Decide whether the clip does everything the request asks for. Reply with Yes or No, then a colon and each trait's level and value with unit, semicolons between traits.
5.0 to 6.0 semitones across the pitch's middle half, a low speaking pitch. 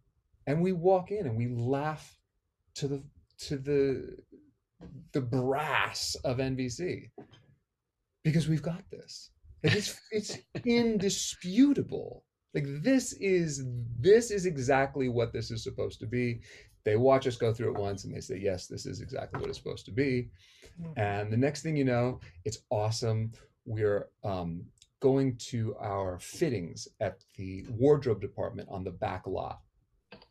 Yes: average, 5.3 semitones; low, 130 Hz